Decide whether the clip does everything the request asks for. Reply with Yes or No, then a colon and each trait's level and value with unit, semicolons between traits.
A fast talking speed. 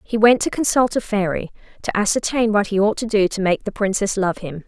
Yes: fast, 245 wpm